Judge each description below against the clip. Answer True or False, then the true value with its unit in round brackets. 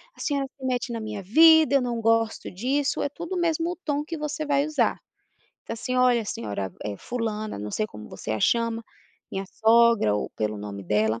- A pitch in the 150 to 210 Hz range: False (230 Hz)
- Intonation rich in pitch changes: True (7.9 semitones)